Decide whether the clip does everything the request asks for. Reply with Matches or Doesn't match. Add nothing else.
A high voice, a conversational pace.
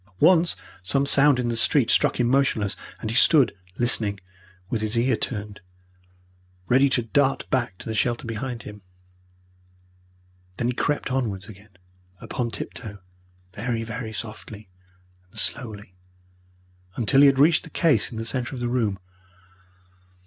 Doesn't match